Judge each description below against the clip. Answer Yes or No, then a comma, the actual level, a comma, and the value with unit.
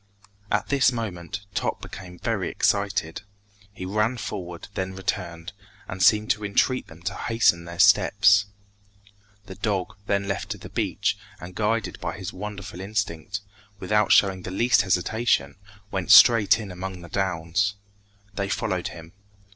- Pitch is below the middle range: Yes, low, 100 Hz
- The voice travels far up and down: No, average, 2.8 semitones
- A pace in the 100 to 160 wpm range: Yes, average, 145 wpm